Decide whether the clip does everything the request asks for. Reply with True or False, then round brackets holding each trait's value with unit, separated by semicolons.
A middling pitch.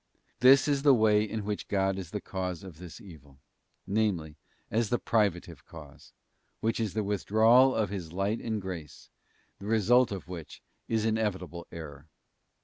False (100 Hz)